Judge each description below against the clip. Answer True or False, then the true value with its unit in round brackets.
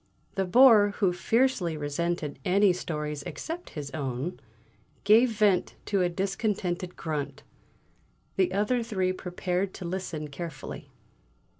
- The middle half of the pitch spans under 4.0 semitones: False (4.4 semitones)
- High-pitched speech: False (180 Hz)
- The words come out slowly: True (120 wpm)